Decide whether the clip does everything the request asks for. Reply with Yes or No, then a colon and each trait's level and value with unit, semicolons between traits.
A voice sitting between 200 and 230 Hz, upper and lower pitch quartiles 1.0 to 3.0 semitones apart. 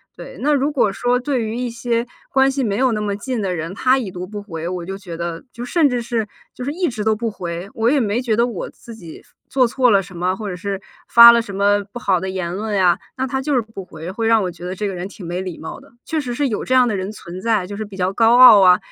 No: high, 215 Hz; average, 4.6 semitones